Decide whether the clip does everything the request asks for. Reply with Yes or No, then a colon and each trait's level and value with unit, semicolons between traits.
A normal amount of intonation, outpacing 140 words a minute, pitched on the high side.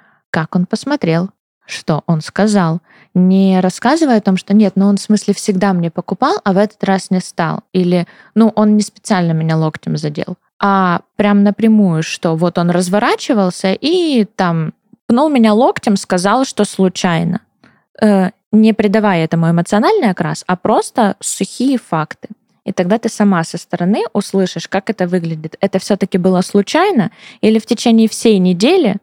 Yes: average, 3.3 semitones; fast, 160 wpm; high, 200 Hz